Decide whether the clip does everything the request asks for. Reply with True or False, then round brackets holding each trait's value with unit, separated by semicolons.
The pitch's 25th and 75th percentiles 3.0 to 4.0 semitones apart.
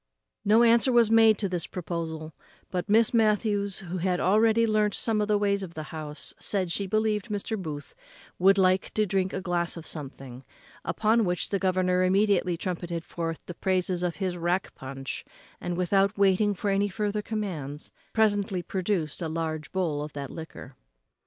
True (3.7 semitones)